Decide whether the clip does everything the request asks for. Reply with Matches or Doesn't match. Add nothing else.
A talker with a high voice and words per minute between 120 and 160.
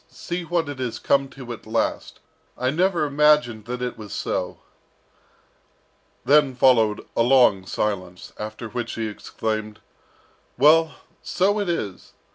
Doesn't match